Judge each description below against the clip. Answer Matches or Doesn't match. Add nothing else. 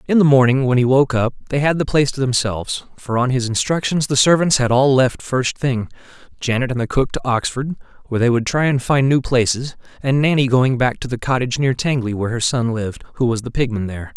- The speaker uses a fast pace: Matches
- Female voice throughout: Doesn't match